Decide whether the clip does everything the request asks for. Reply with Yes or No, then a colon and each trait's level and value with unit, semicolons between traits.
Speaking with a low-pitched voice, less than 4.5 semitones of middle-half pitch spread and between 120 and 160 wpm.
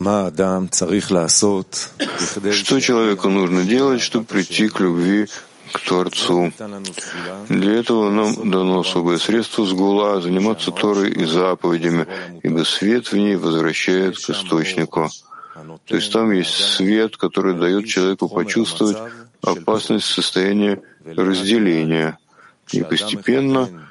No: very low, 95 Hz; average, 2.9 semitones; slow, 110 wpm